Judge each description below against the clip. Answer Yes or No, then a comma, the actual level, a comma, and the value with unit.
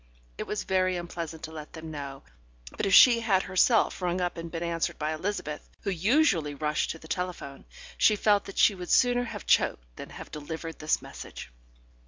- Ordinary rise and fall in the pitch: Yes, average, 4.0 semitones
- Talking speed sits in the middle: Yes, average, 195 wpm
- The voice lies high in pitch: No, medium, 170 Hz